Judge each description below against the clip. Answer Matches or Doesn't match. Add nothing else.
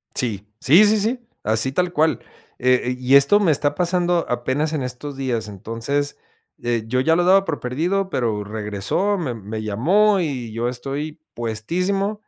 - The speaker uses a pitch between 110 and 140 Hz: Matches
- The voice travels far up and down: Matches